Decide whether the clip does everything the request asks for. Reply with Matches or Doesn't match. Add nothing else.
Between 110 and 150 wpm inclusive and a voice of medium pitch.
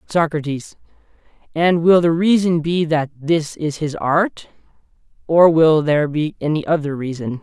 Matches